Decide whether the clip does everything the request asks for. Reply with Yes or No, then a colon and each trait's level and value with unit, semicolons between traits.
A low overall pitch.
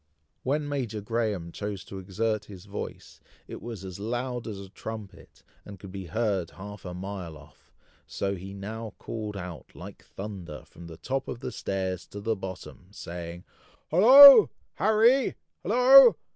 Yes: low, 100 Hz